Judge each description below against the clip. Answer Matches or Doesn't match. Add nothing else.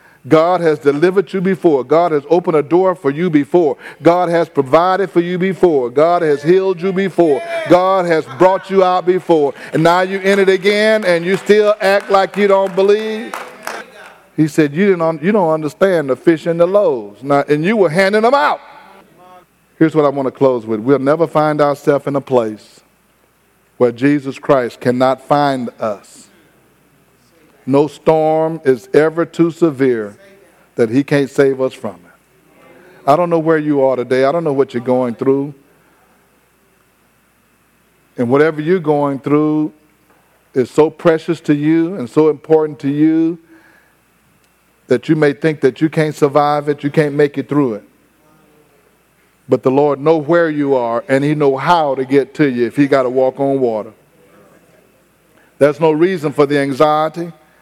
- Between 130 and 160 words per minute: Doesn't match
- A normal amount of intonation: Matches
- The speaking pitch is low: Doesn't match